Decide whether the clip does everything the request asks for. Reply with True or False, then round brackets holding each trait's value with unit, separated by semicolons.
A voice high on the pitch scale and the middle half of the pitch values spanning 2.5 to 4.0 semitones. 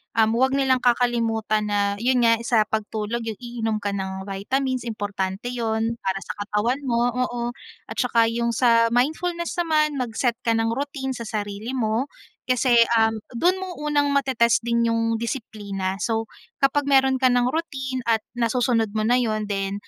True (235 Hz; 2.9 semitones)